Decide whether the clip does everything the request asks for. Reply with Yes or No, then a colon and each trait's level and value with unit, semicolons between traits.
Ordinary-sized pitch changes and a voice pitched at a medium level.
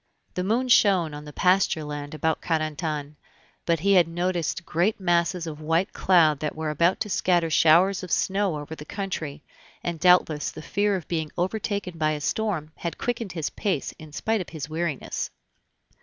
Yes: average, 3.4 semitones; medium, 170 Hz